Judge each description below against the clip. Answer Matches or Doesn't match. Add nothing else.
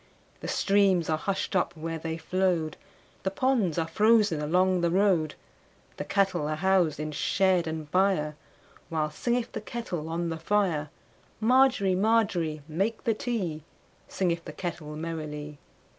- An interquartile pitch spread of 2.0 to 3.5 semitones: Doesn't match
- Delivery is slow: Matches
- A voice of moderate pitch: Matches